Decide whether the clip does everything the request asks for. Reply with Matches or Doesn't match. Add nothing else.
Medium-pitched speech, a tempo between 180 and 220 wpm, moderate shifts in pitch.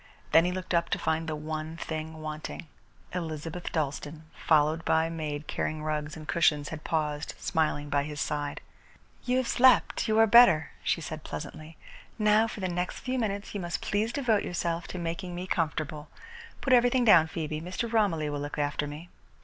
Matches